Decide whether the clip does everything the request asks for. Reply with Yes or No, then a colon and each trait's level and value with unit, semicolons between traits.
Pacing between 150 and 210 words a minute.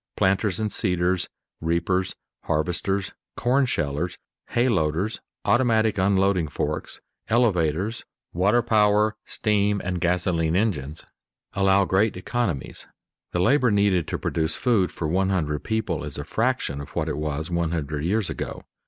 No: slow, 135 wpm